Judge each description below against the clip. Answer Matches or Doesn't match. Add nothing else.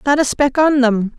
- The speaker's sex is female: Matches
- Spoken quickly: Matches